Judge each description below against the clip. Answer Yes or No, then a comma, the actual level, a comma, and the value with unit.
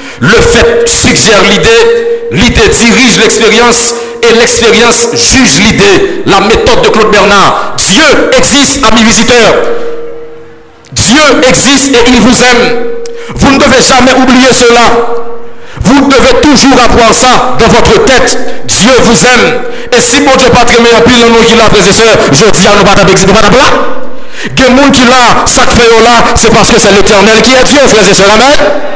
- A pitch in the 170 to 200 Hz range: No, high, 245 Hz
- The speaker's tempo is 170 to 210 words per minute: No, average, 160 wpm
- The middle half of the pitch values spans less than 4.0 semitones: Yes, average, 3.2 semitones